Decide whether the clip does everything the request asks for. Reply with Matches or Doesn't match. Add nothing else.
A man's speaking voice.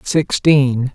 Matches